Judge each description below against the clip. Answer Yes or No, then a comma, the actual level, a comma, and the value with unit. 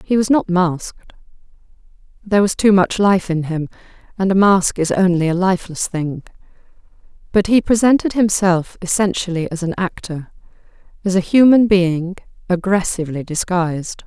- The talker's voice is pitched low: No, medium, 185 Hz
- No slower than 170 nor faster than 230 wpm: No, slow, 135 wpm